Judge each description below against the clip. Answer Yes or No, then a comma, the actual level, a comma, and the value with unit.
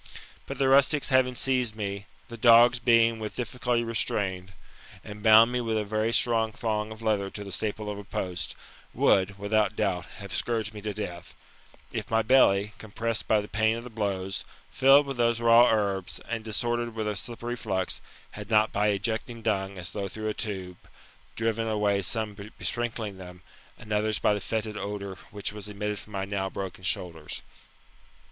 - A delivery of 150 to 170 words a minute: No, average, 180 wpm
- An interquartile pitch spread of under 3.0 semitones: Yes, narrow, 2.4 semitones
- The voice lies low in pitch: Yes, low, 110 Hz